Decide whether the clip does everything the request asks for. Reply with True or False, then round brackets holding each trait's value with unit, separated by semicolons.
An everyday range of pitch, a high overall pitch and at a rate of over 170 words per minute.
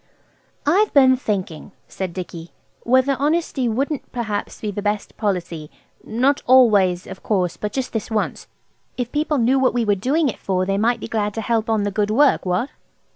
True (4.6 semitones; 225 Hz; 180 wpm)